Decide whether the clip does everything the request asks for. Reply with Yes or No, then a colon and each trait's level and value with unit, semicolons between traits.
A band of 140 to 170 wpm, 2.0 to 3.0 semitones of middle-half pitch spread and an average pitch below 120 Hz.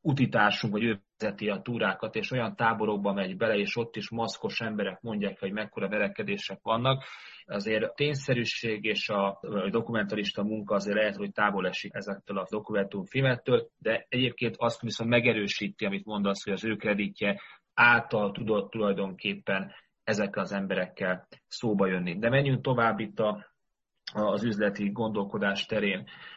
Yes: average, 145 wpm; narrow, 2.5 semitones; low, 105 Hz